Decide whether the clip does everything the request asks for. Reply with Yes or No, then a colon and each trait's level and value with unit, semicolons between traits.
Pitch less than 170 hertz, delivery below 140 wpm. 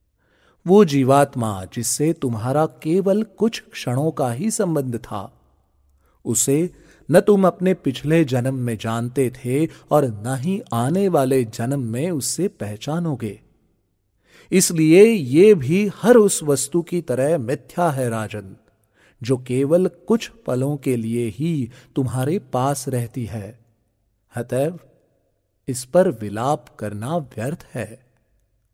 Yes: low, 135 Hz; average, 120 wpm